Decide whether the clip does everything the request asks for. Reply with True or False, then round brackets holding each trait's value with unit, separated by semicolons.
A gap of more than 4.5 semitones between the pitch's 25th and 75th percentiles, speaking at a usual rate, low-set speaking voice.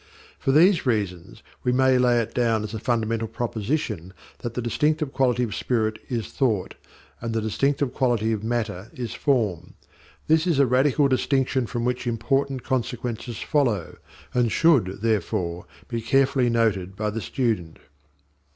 False (3.2 semitones; 150 wpm; 120 Hz)